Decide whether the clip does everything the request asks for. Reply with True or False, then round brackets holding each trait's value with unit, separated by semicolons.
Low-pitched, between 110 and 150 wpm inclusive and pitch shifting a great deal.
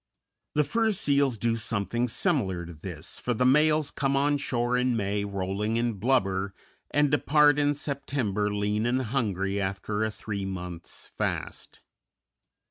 True (115 Hz; 145 wpm; 5.8 semitones)